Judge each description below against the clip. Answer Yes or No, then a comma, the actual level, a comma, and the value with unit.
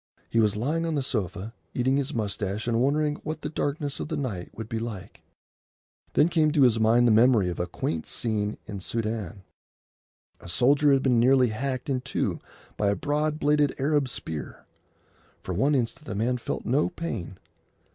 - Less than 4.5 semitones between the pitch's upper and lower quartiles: No, average, 5.1 semitones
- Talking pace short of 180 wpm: No, average, 185 wpm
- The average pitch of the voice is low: Yes, low, 120 Hz